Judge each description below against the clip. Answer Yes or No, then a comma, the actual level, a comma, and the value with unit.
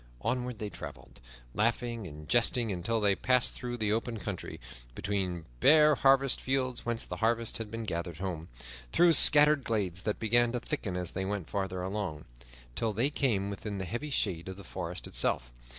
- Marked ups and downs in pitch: No, average, 4.5 semitones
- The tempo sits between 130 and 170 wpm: No, average, 180 wpm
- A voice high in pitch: No, low, 110 Hz